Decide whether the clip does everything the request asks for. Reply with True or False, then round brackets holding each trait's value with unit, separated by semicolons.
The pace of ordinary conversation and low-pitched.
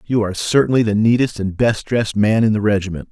False (230 wpm; 110 Hz)